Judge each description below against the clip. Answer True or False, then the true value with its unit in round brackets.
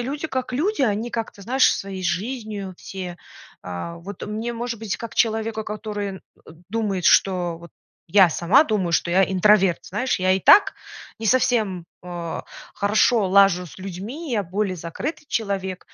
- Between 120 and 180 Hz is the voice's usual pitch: False (205 Hz)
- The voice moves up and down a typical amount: True (3.8 semitones)